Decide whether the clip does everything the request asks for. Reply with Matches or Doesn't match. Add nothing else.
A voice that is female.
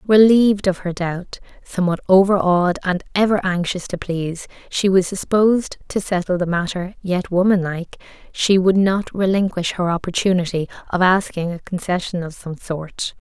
Matches